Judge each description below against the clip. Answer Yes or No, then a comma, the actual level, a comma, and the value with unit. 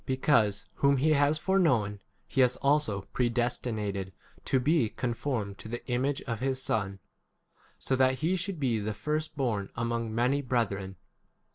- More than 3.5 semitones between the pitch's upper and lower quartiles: Yes, average, 4.5 semitones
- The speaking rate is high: No, average, 160 wpm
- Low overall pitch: Yes, low, 125 Hz